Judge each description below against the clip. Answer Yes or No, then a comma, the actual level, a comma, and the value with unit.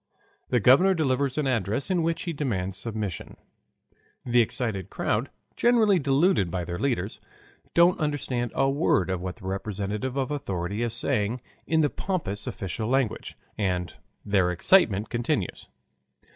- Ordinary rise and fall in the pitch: No, wide, 6.6 semitones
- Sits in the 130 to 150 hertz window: No, low, 120 Hz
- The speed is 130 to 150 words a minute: Yes, average, 145 wpm